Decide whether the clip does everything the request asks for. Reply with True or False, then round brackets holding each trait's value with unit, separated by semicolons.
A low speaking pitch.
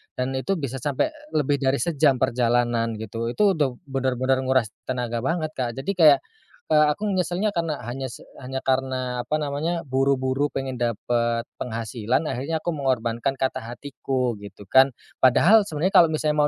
True (130 Hz)